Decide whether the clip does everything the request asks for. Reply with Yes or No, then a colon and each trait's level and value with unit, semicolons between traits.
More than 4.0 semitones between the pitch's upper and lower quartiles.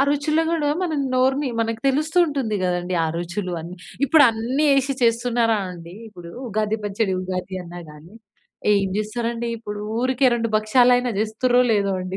Yes: average, 4.9 semitones